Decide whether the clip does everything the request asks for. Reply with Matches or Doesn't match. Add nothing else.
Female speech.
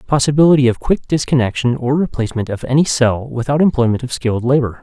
Doesn't match